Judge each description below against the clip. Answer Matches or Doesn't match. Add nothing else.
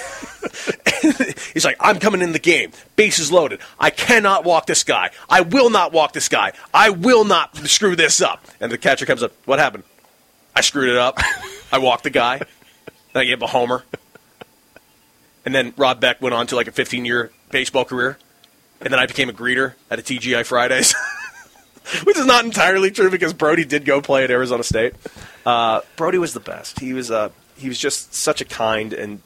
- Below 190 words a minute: Doesn't match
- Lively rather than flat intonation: Matches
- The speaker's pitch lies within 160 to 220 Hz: Doesn't match